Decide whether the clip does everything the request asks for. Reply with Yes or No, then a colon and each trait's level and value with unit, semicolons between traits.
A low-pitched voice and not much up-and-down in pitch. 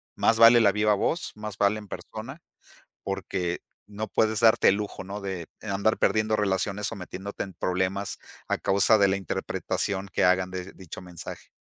Yes: low, 100 Hz; narrow, 2.2 semitones